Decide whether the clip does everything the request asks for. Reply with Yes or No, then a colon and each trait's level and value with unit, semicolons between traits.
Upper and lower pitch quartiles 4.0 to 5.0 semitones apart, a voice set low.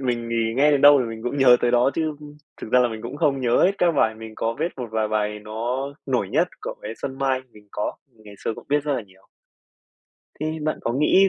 Yes: average, 4.5 semitones; low, 125 Hz